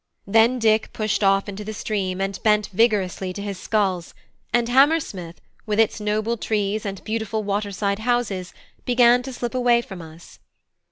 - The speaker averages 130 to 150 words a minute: No, average, 165 wpm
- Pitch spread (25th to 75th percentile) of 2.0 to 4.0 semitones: Yes, average, 2.9 semitones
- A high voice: Yes, high, 210 Hz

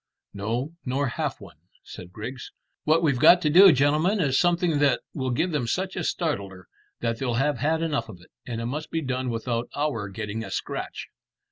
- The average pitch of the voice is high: No, low, 130 Hz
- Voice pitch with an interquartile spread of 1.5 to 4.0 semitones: No, average, 5.2 semitones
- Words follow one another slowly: No, average, 200 wpm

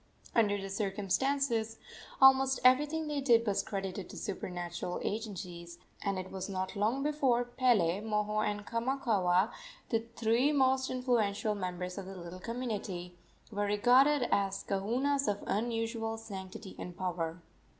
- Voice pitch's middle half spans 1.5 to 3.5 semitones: No, average, 4.5 semitones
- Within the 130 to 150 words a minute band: Yes, slow, 135 wpm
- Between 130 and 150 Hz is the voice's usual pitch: No, high, 210 Hz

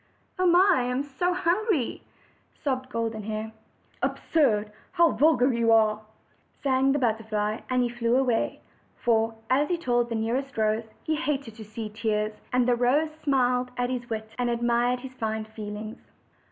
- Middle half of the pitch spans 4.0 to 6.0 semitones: No, average, 3.4 semitones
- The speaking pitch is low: No, high, 240 Hz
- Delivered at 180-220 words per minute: No, average, 160 wpm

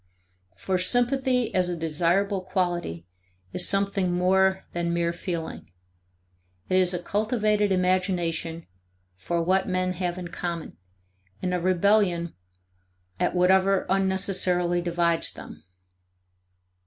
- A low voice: No, medium, 185 Hz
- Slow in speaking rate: Yes, slow, 110 wpm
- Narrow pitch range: Yes, narrow, 1.8 semitones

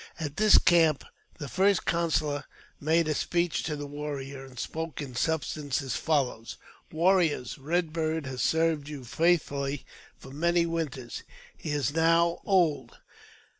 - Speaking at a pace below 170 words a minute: Yes, average, 140 wpm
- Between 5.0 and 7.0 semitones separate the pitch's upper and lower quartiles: No, average, 3.0 semitones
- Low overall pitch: No, medium, 155 Hz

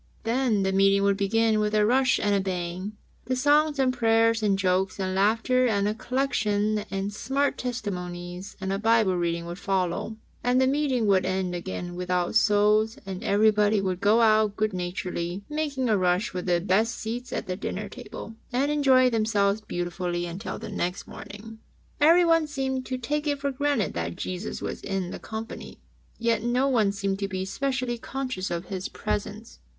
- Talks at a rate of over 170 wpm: Yes, average, 180 wpm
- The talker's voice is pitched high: Yes, high, 210 Hz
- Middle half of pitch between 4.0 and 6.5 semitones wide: Yes, average, 4.7 semitones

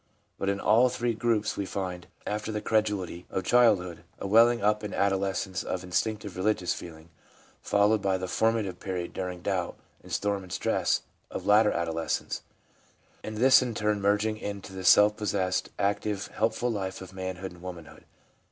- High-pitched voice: No, low, 100 Hz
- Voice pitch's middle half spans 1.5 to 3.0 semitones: Yes, narrow, 2.6 semitones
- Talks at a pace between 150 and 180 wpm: Yes, average, 170 wpm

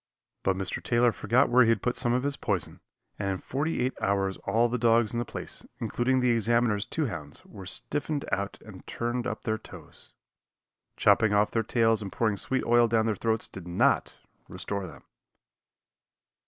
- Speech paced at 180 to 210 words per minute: Yes, average, 185 wpm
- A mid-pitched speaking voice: No, low, 115 Hz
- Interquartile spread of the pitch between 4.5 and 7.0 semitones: No, average, 3.2 semitones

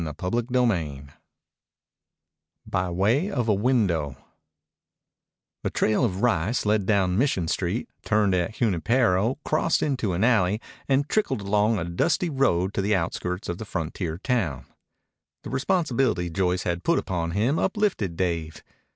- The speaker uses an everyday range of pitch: No, wide, 5.8 semitones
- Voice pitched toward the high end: No, low, 100 Hz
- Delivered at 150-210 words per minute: No, average, 140 wpm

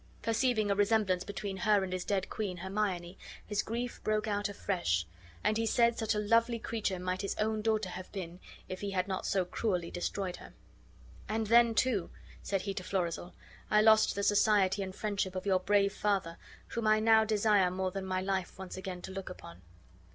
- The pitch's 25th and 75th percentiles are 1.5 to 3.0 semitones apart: Yes, narrow, 2.5 semitones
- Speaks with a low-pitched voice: No, high, 200 Hz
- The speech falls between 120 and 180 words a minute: No, average, 195 wpm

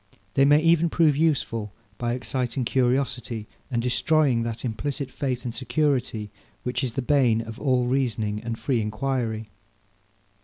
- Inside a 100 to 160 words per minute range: Yes, average, 145 wpm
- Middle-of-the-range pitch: No, low, 125 Hz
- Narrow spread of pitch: No, average, 3.2 semitones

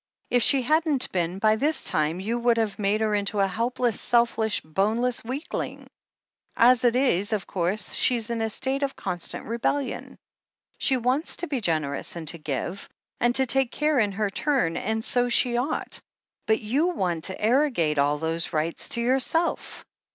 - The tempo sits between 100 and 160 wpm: No, average, 180 wpm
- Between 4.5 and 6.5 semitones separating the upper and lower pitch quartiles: Yes, average, 4.9 semitones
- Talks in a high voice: Yes, high, 225 Hz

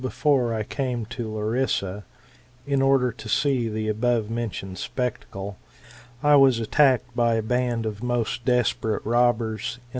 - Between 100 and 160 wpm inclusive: Yes, average, 150 wpm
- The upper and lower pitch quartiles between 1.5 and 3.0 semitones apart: Yes, narrow, 2.6 semitones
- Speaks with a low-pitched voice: Yes, low, 120 Hz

